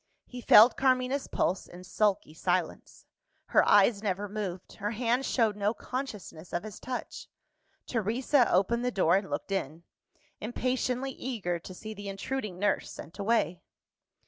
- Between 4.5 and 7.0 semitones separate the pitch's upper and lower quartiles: Yes, average, 4.8 semitones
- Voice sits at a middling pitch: No, high, 210 Hz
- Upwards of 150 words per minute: No, average, 145 wpm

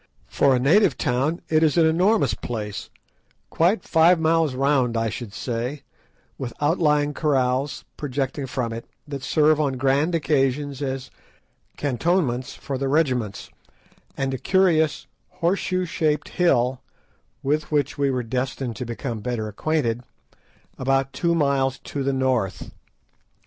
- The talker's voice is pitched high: No, medium, 140 Hz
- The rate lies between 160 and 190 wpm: No, slow, 135 wpm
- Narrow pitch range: No, average, 3.7 semitones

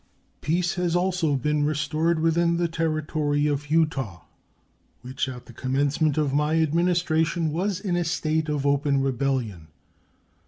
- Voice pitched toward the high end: No, medium, 155 Hz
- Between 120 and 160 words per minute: Yes, average, 140 wpm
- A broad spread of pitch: No, average, 3.0 semitones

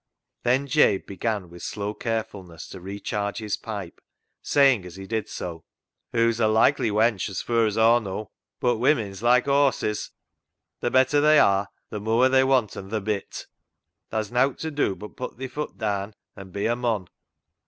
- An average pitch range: Yes, average, 3.7 semitones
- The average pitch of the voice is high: No, low, 110 Hz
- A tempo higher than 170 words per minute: Yes, average, 185 wpm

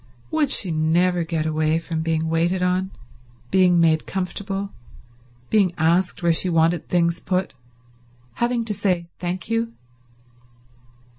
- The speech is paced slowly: Yes, slow, 130 wpm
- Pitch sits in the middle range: Yes, medium, 175 Hz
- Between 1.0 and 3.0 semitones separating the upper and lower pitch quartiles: Yes, narrow, 2.6 semitones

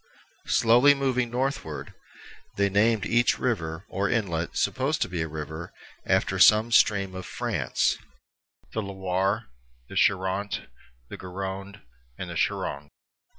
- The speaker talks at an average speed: No, slow, 120 wpm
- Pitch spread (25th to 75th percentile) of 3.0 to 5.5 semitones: Yes, average, 4.2 semitones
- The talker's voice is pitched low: Yes, low, 100 Hz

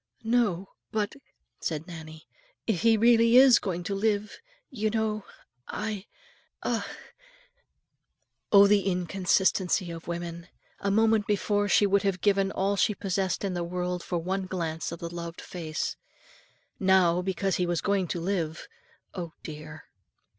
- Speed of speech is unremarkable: Yes, average, 150 wpm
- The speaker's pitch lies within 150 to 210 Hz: Yes, high, 190 Hz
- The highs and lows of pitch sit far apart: No, average, 3.1 semitones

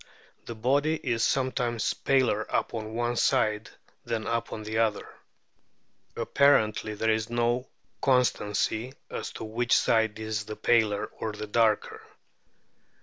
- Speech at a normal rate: No, slow, 125 wpm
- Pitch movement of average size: No, narrow, 1.9 semitones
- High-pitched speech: No, low, 115 Hz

